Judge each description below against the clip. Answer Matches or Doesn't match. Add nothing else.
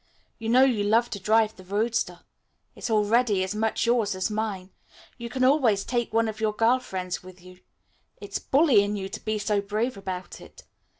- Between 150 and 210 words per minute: Matches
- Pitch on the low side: Doesn't match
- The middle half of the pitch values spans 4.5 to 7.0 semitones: Doesn't match